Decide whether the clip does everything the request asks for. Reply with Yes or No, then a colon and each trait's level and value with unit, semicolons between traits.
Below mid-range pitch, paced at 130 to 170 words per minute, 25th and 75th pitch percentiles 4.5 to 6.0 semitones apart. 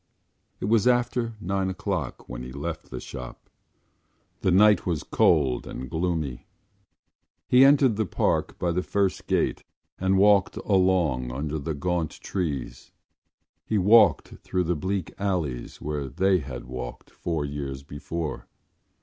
Yes: very low, 85 Hz; average, 140 wpm; wide, 5.5 semitones